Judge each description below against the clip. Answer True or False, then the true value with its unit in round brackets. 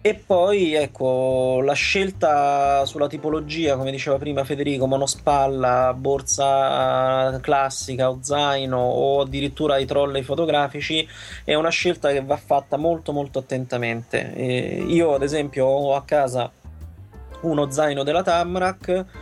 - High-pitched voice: False (140 Hz)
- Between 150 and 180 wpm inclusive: False (130 wpm)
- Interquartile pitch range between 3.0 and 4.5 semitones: False (2.5 semitones)